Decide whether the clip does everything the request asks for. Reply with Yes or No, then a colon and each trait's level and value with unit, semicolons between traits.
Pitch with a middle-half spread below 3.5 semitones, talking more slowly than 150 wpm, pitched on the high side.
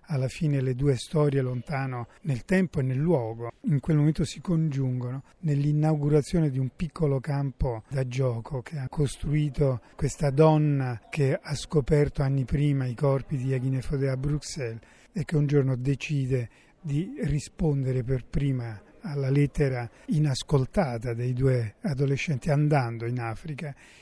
No: narrow, 2.5 semitones; average, 140 wpm; medium, 140 Hz